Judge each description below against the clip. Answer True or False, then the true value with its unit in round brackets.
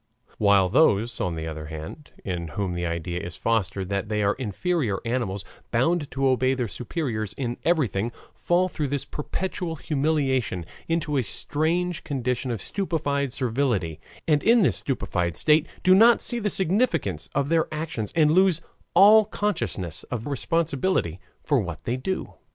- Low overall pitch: True (130 Hz)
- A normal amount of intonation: False (8.5 semitones)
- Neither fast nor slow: True (155 wpm)